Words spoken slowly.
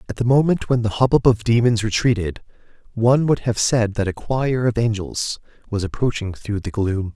No: average, 195 wpm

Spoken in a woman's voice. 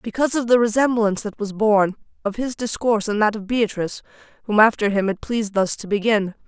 Yes: female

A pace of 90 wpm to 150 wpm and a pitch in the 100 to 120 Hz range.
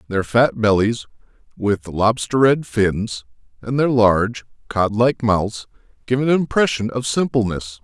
Yes: average, 145 wpm; low, 115 Hz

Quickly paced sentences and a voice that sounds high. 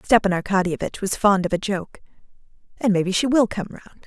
No: average, 190 wpm; high, 200 Hz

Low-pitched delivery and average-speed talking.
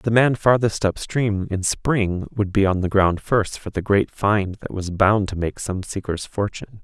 No: low, 100 Hz; fast, 210 wpm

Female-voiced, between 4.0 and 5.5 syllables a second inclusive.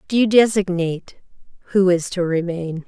Yes: female; 5.0 syllables/s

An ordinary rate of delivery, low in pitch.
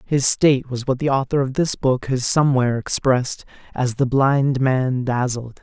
Yes: average, 180 wpm; low, 130 Hz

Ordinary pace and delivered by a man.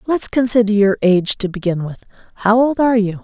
No: average, 185 wpm; female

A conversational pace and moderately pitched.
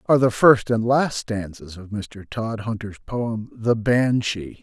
No: average, 155 wpm; low, 110 Hz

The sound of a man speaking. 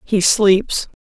No: female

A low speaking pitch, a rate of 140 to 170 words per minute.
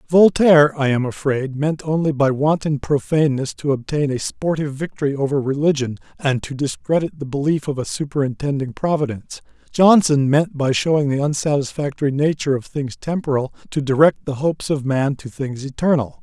No: medium, 145 Hz; average, 165 wpm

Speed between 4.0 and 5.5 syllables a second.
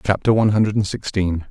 No: 5.8 syllables/s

